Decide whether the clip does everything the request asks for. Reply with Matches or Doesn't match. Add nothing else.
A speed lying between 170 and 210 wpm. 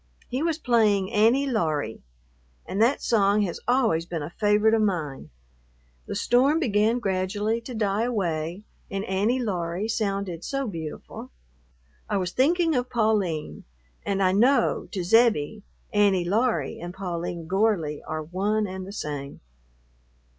Doesn't match